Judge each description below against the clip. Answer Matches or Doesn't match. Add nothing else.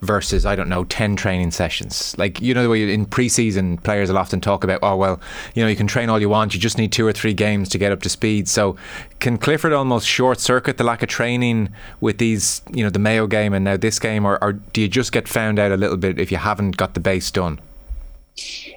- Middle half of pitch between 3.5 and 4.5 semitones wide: Doesn't match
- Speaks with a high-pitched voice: Doesn't match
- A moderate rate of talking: Doesn't match